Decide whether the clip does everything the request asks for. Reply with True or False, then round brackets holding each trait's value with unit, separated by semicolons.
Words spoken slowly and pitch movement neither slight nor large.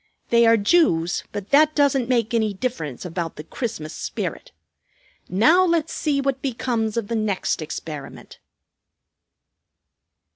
False (125 wpm; 6.6 semitones)